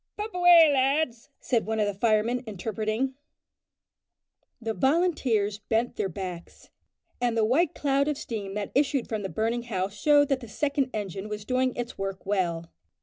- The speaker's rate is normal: Yes, average, 165 wpm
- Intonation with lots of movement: No, average, 4.8 semitones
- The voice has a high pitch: Yes, high, 230 Hz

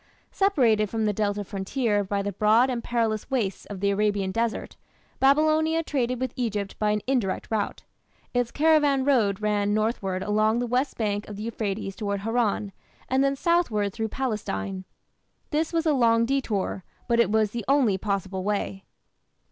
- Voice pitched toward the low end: No, high, 220 Hz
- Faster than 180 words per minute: No, average, 165 wpm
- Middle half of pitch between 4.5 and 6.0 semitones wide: No, average, 4.1 semitones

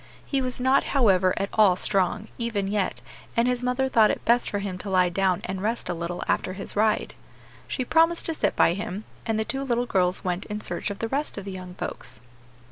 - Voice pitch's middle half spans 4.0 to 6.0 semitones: Yes, average, 4.7 semitones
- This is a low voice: No, high, 210 Hz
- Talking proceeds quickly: Yes, fast, 225 wpm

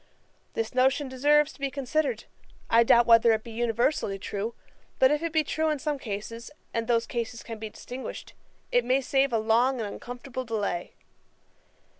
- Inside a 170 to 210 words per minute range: Yes, average, 175 wpm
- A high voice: Yes, high, 245 Hz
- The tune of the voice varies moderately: Yes, average, 3.4 semitones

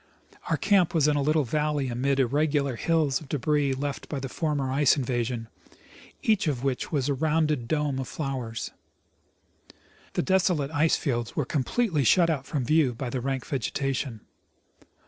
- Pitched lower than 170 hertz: Yes, medium, 140 Hz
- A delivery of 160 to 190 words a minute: Yes, average, 165 wpm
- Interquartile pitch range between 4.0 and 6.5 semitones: No, average, 2.7 semitones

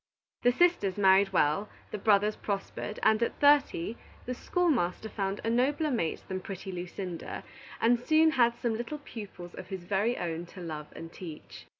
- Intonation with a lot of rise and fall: No, average, 5.0 semitones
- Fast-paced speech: No, average, 170 wpm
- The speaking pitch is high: Yes, high, 205 Hz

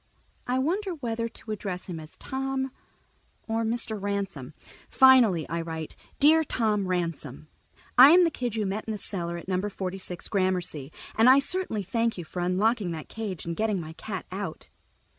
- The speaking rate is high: No, average, 180 wpm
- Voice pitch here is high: Yes, high, 205 Hz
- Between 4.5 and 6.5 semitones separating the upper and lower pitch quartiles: Yes, average, 5.0 semitones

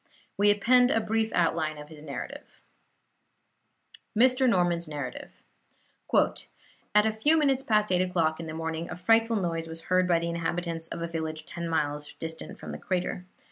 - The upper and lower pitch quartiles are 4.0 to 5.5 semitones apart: Yes, average, 4.8 semitones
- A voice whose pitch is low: No, medium, 170 Hz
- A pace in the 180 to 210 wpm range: No, average, 170 wpm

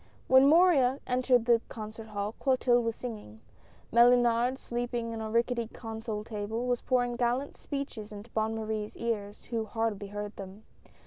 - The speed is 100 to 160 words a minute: Yes, average, 150 wpm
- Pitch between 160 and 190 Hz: No, high, 230 Hz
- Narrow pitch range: Yes, narrow, 2.3 semitones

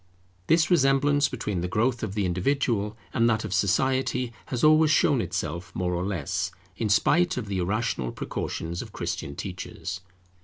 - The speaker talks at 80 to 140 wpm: No, average, 160 wpm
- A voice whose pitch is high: No, low, 110 Hz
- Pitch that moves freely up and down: Yes, wide, 6.4 semitones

